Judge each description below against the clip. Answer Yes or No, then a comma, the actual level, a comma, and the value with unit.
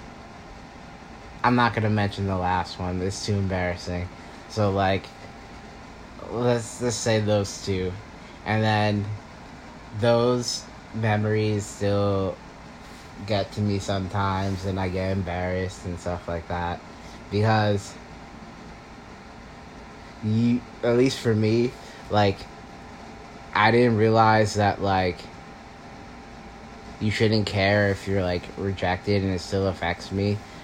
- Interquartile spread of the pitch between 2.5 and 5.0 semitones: Yes, average, 2.9 semitones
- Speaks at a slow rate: Yes, slow, 115 wpm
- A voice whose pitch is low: Yes, low, 100 Hz